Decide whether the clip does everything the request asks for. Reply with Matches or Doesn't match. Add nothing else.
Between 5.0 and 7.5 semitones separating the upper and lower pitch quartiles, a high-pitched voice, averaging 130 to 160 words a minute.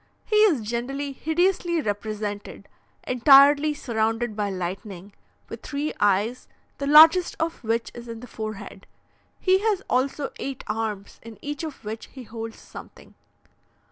Matches